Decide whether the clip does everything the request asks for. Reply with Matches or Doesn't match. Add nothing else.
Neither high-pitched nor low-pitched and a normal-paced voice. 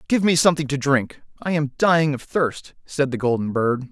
Doesn't match